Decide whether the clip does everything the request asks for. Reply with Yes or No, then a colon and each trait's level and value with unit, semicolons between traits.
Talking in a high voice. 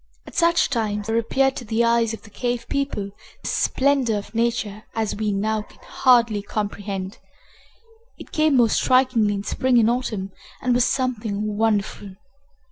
Yes: high, 225 Hz